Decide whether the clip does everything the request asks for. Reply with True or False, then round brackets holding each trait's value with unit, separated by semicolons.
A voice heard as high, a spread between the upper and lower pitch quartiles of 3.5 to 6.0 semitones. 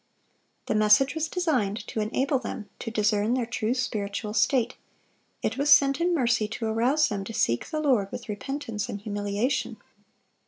True (225 Hz; 4.5 semitones)